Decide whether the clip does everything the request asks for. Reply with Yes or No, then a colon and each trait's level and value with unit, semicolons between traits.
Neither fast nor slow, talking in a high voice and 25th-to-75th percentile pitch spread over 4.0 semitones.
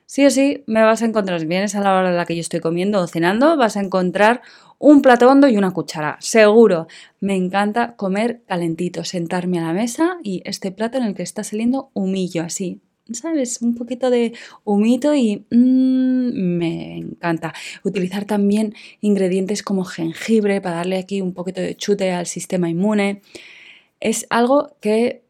Yes: average, 180 wpm; high, 205 Hz; average, 4.7 semitones